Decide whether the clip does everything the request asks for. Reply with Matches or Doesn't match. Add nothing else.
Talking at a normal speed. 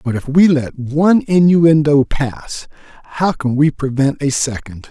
Matches